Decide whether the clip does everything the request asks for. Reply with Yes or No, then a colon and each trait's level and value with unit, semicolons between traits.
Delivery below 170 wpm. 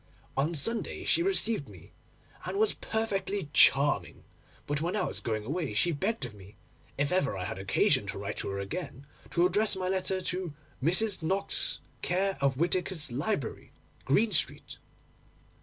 Yes: average, 160 wpm